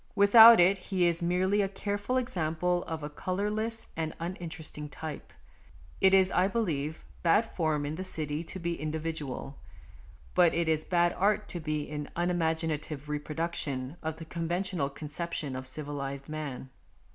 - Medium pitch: Yes, medium, 165 Hz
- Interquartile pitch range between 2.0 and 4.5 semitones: Yes, average, 3.5 semitones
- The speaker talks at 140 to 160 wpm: Yes, average, 150 wpm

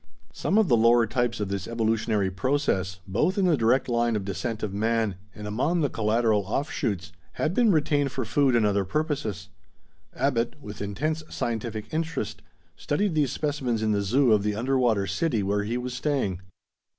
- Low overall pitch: Yes, low, 115 Hz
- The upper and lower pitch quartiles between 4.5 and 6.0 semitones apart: Yes, average, 5.2 semitones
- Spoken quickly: No, average, 175 wpm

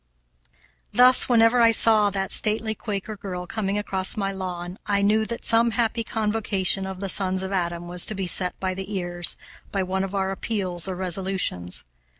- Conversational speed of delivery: Yes, average, 180 wpm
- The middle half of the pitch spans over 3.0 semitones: No, average, 2.7 semitones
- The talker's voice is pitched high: Yes, high, 195 Hz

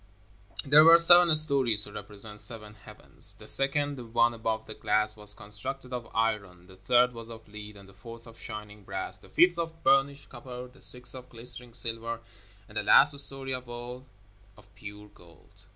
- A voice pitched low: Yes, low, 115 Hz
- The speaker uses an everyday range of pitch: Yes, average, 3.8 semitones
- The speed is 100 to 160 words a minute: No, average, 185 wpm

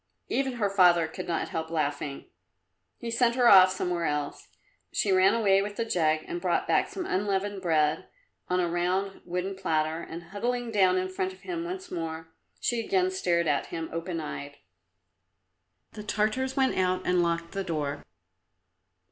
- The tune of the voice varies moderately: Yes, average, 3.6 semitones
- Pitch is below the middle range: No, medium, 185 Hz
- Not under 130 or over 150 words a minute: No, average, 170 wpm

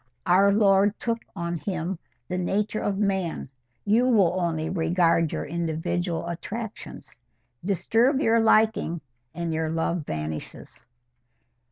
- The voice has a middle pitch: Yes, medium, 180 Hz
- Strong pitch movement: No, average, 4.0 semitones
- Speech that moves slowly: Yes, slow, 120 wpm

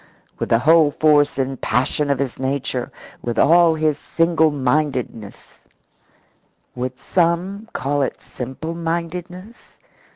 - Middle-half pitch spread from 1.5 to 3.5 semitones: No, average, 4.2 semitones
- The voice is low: No, medium, 150 Hz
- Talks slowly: Yes, slow, 120 wpm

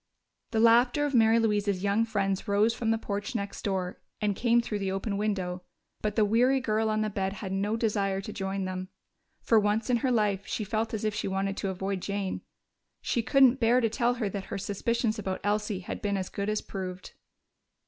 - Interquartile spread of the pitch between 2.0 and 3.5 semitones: Yes, narrow, 2.5 semitones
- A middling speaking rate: No, fast, 210 wpm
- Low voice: No, high, 210 Hz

